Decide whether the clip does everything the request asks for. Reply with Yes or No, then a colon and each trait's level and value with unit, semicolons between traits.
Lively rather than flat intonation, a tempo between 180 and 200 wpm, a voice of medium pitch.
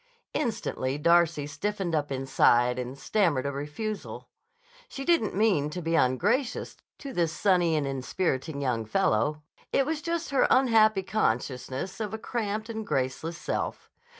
No: wide, 8.0 semitones; average, 145 wpm; medium, 170 Hz